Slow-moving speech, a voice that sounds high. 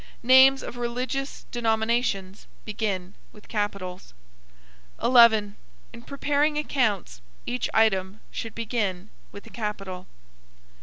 Yes: slow, 100 wpm; high, 220 Hz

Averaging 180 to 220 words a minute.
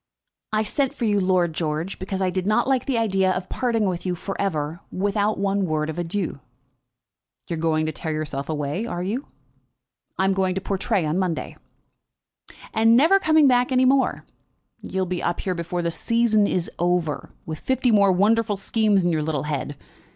Yes: average, 190 wpm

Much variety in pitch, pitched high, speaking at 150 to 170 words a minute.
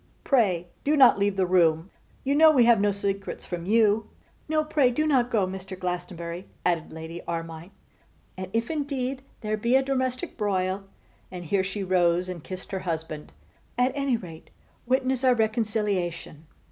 Yes: wide, 5.9 semitones; high, 200 Hz; average, 165 wpm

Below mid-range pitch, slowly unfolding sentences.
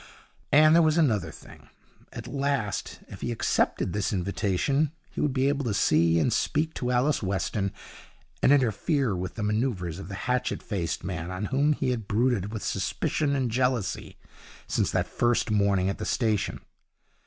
No: low, 115 Hz; average, 170 wpm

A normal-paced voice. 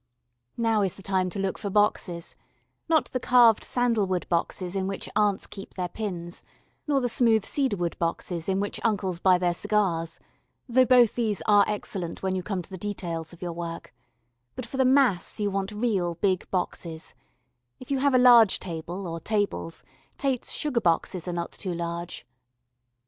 Yes: average, 180 wpm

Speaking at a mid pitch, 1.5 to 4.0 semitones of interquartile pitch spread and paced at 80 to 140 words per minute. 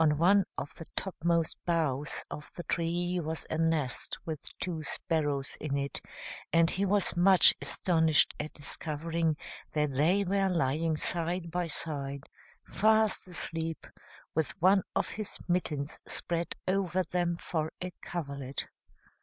Yes: medium, 165 Hz; average, 2.9 semitones; slow, 135 wpm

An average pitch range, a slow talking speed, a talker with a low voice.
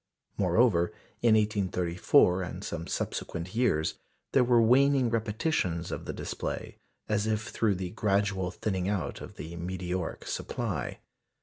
Yes: average, 3.9 semitones; slow, 130 wpm; low, 100 Hz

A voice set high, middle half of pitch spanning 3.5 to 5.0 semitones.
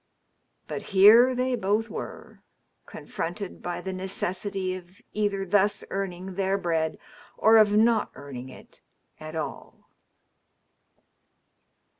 No: high, 195 Hz; average, 2.9 semitones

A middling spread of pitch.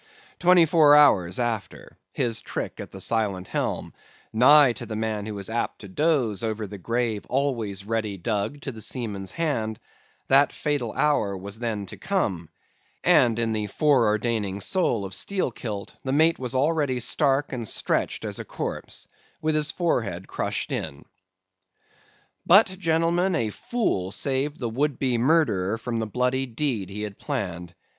No: wide, 5.9 semitones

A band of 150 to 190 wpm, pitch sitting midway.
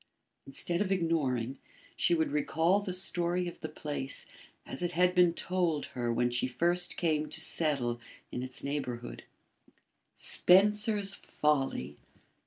No: slow, 135 wpm; medium, 160 Hz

